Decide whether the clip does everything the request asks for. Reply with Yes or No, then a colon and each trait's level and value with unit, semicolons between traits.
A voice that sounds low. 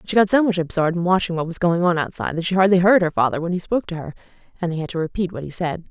No: medium, 175 Hz